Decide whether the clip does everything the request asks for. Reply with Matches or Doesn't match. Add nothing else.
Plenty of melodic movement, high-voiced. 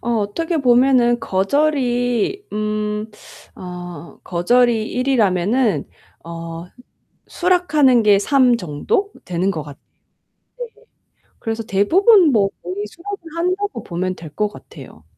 Matches